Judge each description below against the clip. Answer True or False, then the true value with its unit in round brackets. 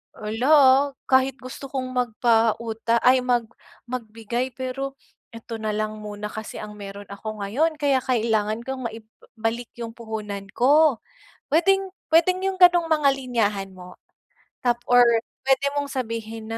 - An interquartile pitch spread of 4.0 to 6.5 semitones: False (3.5 semitones)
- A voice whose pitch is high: True (235 Hz)